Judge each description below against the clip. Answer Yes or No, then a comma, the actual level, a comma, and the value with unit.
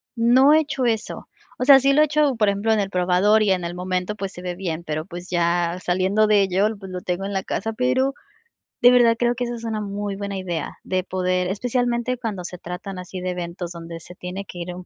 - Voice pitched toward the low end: No, high, 195 Hz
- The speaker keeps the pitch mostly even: No, average, 4.3 semitones